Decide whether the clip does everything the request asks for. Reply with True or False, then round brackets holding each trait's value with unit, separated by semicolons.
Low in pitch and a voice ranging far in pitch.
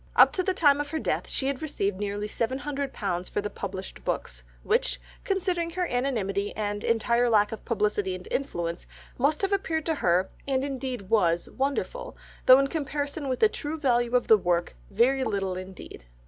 False (245 Hz; 6.2 semitones)